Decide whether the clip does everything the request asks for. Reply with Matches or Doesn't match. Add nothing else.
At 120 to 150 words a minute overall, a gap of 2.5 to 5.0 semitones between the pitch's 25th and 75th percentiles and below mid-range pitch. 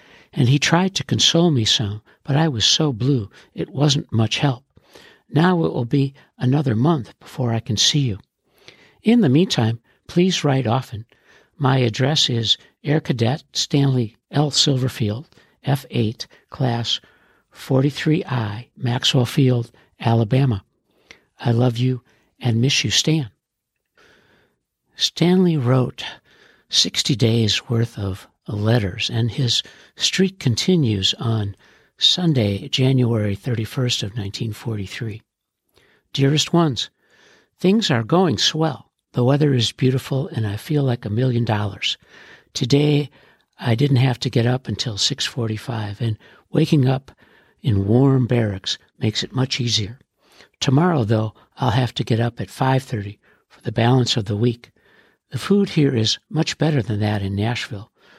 Matches